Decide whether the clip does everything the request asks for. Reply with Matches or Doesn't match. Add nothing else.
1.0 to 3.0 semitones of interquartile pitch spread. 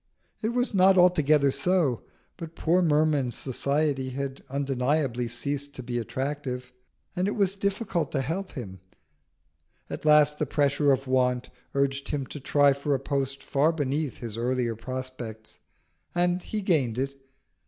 Doesn't match